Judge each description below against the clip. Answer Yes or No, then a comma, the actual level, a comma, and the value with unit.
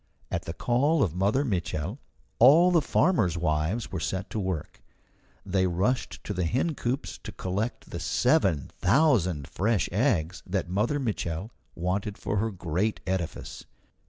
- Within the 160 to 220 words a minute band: No, average, 145 wpm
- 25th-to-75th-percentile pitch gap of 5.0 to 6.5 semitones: Yes, wide, 5.4 semitones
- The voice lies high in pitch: No, low, 100 Hz